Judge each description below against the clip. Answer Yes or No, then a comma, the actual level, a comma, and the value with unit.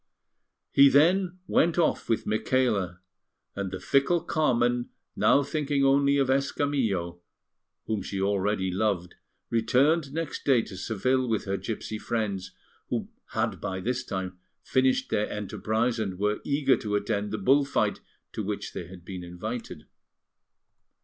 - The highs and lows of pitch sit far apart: Yes, wide, 6.0 semitones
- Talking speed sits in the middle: Yes, average, 145 wpm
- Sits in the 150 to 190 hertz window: No, low, 110 Hz